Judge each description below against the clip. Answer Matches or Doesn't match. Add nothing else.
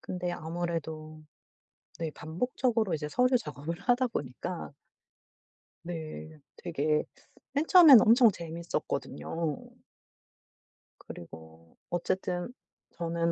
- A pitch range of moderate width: Matches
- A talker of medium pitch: Matches